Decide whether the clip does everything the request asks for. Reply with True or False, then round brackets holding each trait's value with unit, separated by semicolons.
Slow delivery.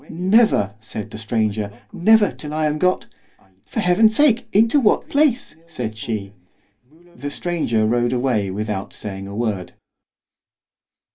True (125 wpm)